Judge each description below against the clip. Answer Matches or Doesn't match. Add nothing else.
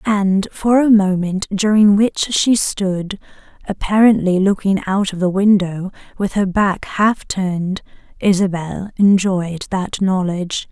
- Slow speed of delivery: Matches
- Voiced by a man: Doesn't match